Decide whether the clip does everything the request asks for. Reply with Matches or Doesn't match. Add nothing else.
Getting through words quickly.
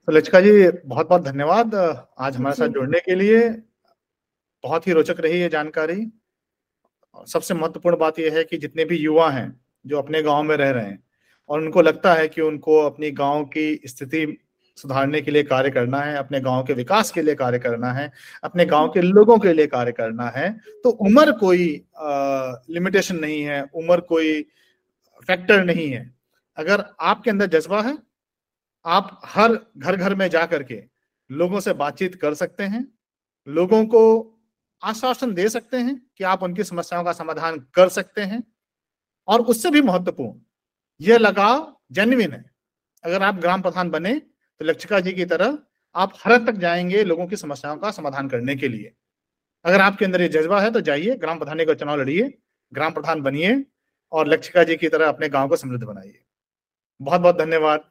Doesn't match